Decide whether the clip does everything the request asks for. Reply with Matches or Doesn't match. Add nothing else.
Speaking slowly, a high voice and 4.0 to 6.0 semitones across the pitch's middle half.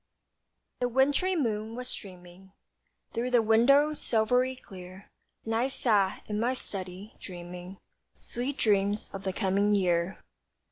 Matches